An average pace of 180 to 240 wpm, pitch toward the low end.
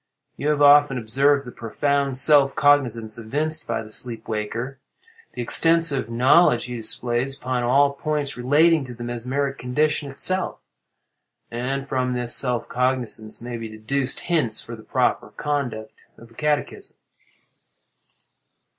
No: slow, 135 wpm; low, 130 Hz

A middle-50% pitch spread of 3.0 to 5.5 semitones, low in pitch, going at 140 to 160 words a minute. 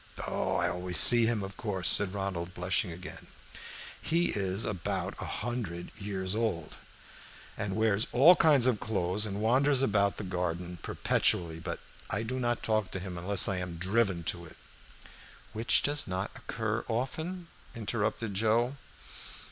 Yes: average, 4.3 semitones; low, 100 Hz; average, 155 wpm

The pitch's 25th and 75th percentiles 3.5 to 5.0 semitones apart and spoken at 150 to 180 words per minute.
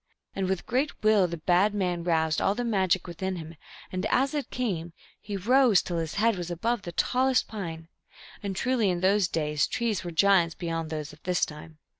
No: average, 4.4 semitones; average, 200 wpm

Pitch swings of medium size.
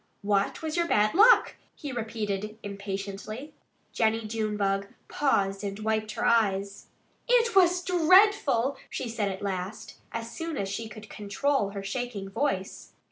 No: wide, 5.9 semitones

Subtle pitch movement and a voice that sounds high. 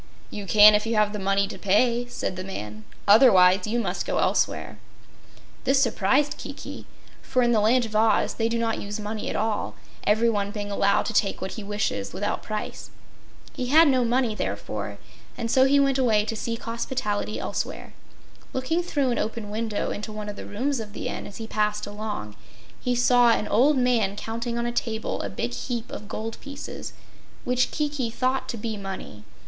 No: average, 3.0 semitones; high, 225 Hz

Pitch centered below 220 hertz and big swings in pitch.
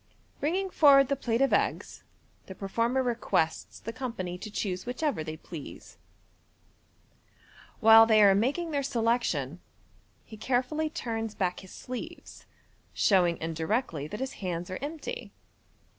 No: high, 230 Hz; wide, 6.6 semitones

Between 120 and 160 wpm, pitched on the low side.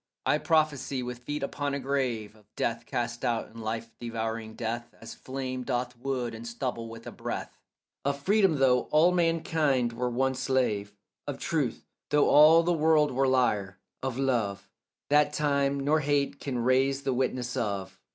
No: average, 170 wpm; low, 130 Hz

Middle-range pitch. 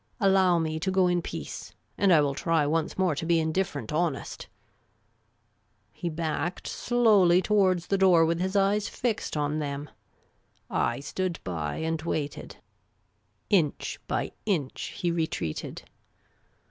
Yes: medium, 170 Hz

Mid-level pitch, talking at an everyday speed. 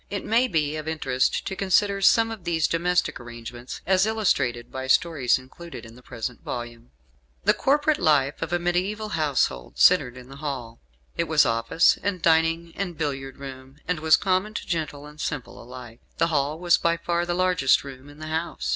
Yes: medium, 155 Hz; average, 190 wpm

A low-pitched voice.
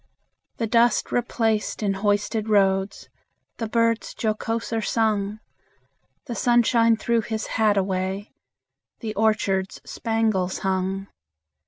No: high, 215 Hz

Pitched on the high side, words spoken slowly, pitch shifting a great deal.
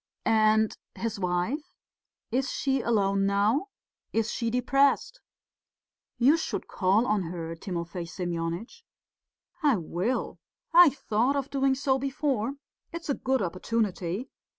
Yes: high, 225 Hz; slow, 120 wpm; wide, 6.1 semitones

